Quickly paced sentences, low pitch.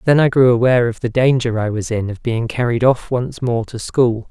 Yes: fast, 250 wpm; low, 120 Hz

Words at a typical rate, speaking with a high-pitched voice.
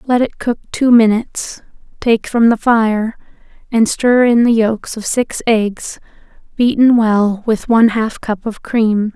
Yes: average, 165 wpm; high, 225 Hz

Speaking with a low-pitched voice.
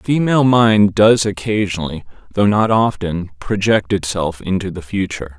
Yes: low, 100 Hz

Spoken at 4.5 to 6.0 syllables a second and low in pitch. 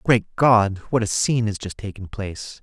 Yes: 5.1 syllables/s; low, 105 Hz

